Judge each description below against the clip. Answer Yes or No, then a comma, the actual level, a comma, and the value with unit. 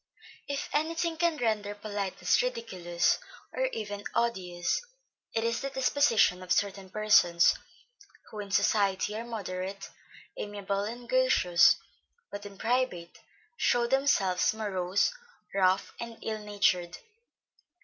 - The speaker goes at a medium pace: No, slow, 120 wpm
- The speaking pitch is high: Yes, high, 205 Hz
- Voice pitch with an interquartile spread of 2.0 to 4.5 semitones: Yes, average, 3.9 semitones